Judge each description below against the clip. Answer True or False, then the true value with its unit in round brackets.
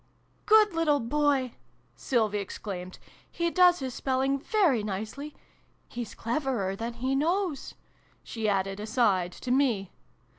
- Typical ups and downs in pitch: False (6.0 semitones)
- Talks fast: False (145 wpm)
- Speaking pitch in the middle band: False (250 Hz)